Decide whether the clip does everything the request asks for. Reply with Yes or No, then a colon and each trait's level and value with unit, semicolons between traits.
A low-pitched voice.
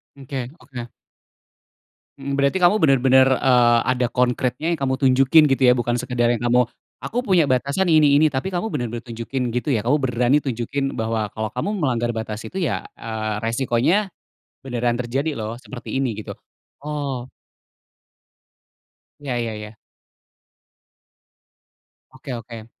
Yes: low, 125 Hz